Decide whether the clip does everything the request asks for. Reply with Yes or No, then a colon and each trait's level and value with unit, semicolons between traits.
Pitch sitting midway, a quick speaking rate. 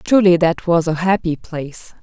No: medium, 170 Hz; average, 180 wpm